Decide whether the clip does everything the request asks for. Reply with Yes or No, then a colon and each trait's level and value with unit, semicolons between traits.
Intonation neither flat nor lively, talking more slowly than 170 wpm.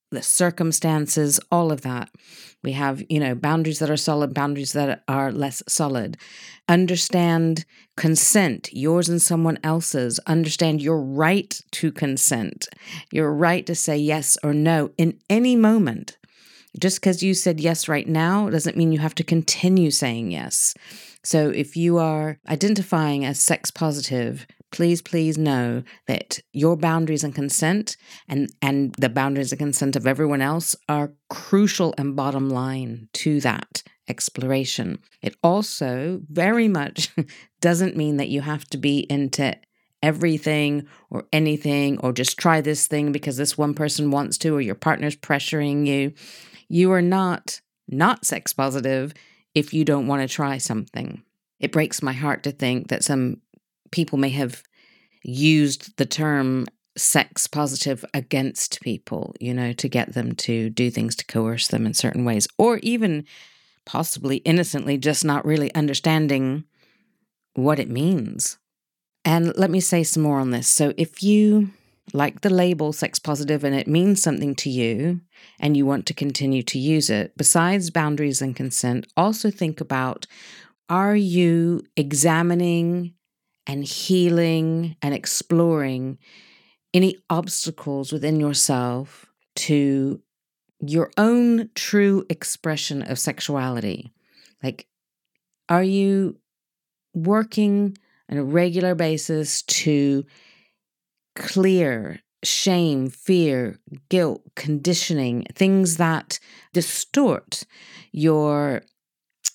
Yes: average, 3.6 semitones; slow, 135 wpm